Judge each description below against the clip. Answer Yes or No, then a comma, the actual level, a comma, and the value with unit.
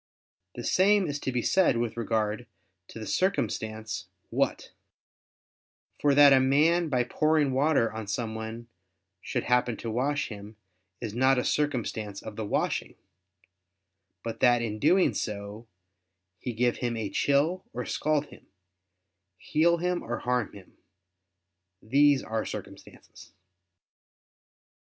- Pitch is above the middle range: No, low, 125 Hz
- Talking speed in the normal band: No, slow, 130 wpm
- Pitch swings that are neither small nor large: Yes, average, 4.8 semitones